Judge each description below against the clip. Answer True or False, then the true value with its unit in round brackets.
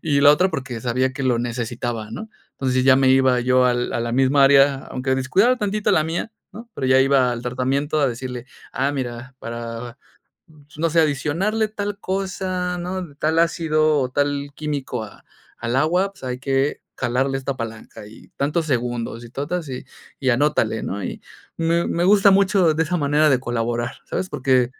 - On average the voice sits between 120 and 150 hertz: True (135 Hz)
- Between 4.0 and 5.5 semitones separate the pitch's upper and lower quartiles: True (4.7 semitones)